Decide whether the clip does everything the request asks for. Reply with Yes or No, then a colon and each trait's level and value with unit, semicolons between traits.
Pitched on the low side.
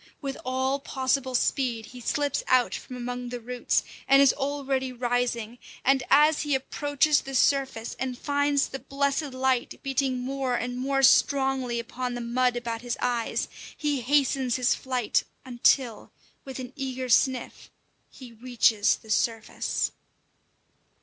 No: very high, 255 Hz